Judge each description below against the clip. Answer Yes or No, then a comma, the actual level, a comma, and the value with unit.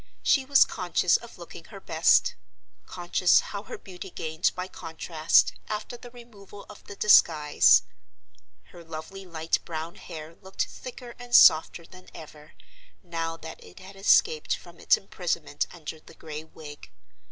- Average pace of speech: Yes, average, 150 wpm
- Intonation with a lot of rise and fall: No, average, 3.9 semitones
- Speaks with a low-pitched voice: No, medium, 170 Hz